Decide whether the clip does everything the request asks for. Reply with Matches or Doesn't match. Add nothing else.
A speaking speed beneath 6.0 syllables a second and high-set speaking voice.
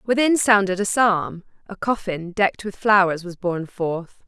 Matches